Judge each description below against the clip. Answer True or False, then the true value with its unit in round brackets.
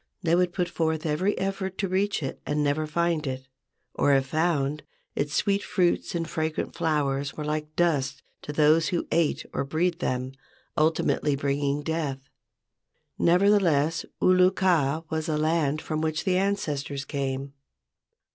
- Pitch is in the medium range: True (155 Hz)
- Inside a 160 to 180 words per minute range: False (150 wpm)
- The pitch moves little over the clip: False (3.4 semitones)